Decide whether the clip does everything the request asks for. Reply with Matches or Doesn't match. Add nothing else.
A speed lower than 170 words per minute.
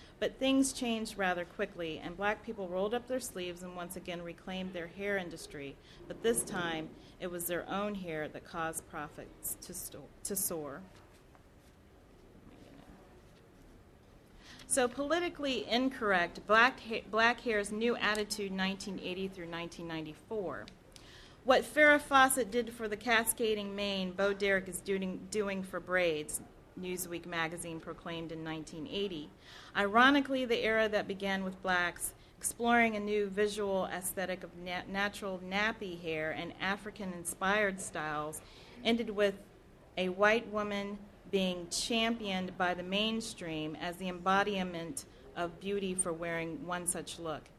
Matches